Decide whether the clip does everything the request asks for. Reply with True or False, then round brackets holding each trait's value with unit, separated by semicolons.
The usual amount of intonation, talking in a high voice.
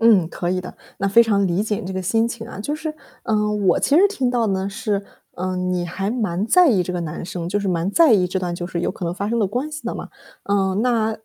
True (3.9 semitones; 200 Hz)